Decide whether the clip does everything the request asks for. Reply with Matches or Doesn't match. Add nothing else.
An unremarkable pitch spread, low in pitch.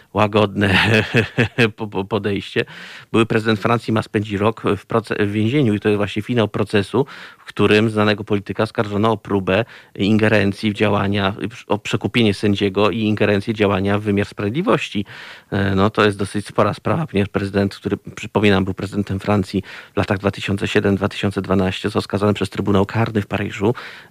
Doesn't match